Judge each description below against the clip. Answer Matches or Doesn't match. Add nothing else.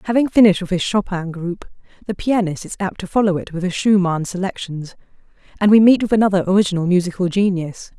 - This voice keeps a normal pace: Matches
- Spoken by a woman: Matches